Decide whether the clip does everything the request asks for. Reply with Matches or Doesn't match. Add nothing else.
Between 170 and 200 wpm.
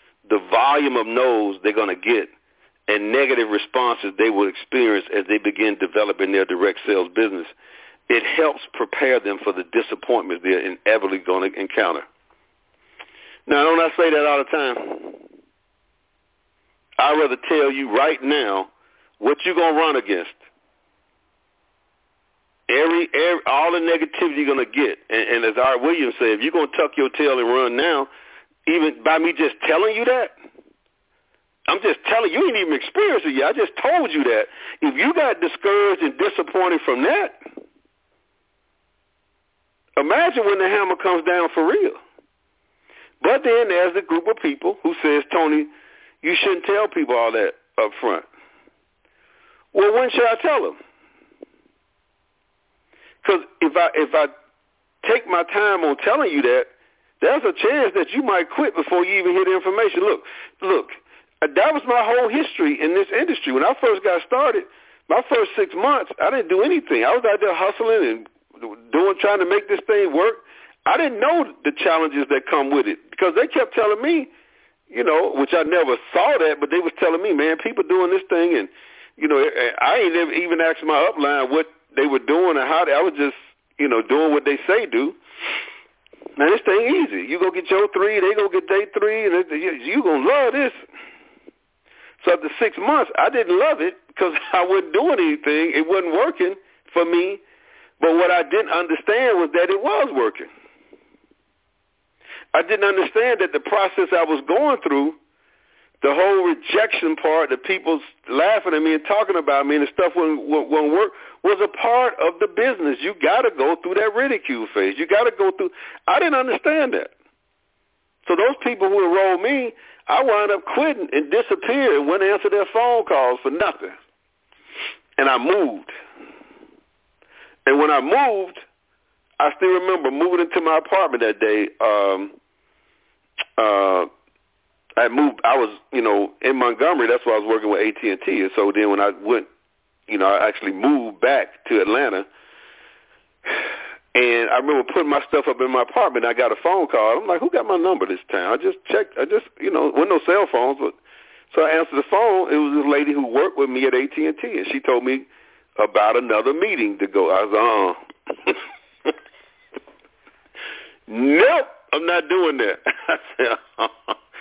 Matches